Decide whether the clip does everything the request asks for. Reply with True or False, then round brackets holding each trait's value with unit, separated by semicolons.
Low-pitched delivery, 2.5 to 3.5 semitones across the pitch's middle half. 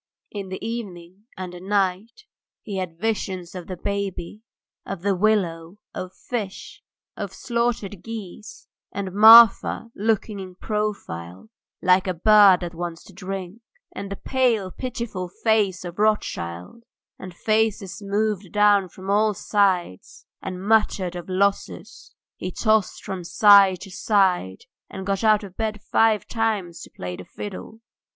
False (195 Hz; 2.9 semitones)